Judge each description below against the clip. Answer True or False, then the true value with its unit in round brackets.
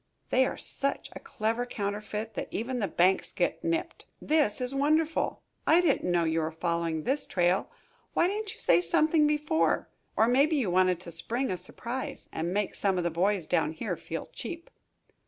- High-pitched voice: True (215 Hz)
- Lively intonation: True (8.6 semitones)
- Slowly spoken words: False (185 wpm)